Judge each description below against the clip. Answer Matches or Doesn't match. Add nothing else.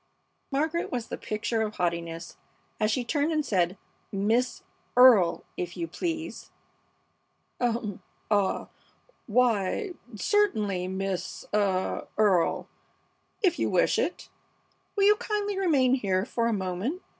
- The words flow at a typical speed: Doesn't match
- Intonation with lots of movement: Matches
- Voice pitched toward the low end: Doesn't match